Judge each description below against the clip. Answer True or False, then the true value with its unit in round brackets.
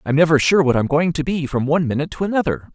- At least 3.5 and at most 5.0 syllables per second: False (7.3 syllables/s)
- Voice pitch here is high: False (155 Hz)